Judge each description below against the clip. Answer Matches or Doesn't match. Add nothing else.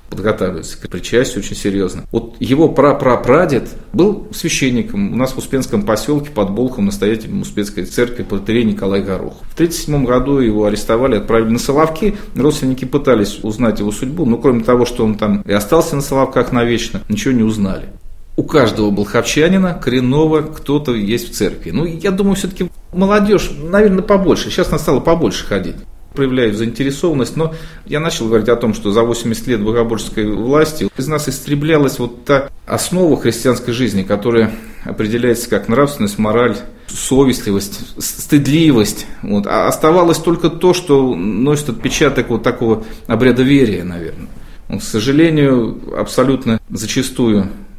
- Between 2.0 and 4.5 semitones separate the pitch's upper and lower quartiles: Doesn't match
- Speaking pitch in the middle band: Doesn't match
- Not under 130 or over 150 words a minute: Matches